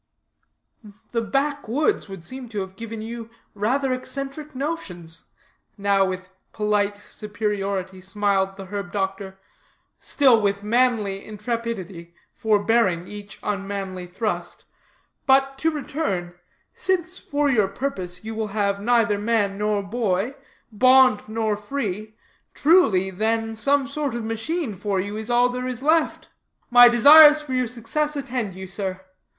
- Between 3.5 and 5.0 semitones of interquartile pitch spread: Yes, average, 4.5 semitones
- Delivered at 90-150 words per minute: Yes, slow, 135 wpm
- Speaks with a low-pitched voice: No, high, 220 Hz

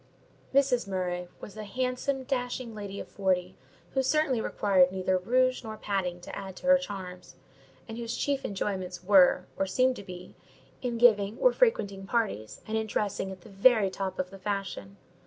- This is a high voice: Yes, high, 200 Hz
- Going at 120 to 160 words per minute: No, average, 175 wpm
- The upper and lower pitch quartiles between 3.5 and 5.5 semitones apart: Yes, average, 4.8 semitones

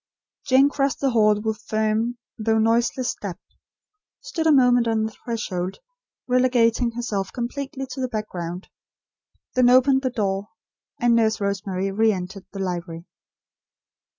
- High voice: Yes, high, 225 Hz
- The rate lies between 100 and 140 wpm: Yes, slow, 135 wpm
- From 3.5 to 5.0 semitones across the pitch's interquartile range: Yes, average, 3.9 semitones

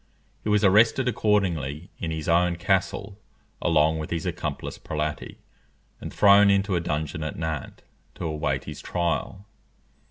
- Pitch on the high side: No, very low, 85 Hz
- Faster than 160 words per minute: No, average, 140 wpm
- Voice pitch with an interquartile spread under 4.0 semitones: No, average, 4.3 semitones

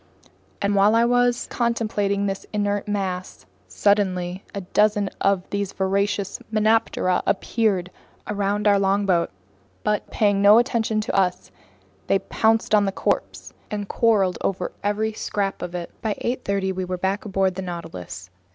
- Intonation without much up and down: Yes, narrow, 1.9 semitones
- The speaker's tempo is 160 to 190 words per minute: No, average, 145 wpm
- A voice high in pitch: Yes, high, 200 Hz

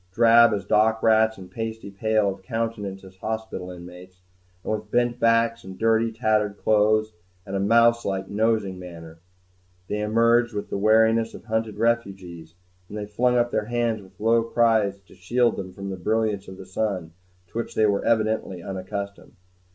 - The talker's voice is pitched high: No, low, 110 Hz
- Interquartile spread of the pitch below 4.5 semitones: Yes, average, 2.8 semitones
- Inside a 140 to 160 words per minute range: No, average, 175 wpm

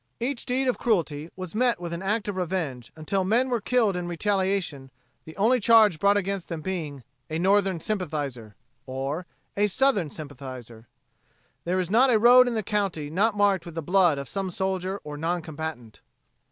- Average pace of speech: Yes, average, 180 wpm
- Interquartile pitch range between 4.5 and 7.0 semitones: Yes, average, 4.9 semitones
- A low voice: No, medium, 185 Hz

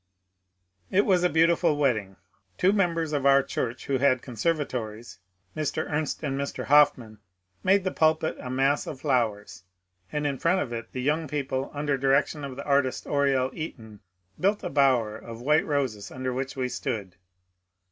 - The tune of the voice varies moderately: Yes, average, 3.2 semitones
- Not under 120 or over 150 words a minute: No, average, 165 wpm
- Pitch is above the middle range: No, medium, 140 Hz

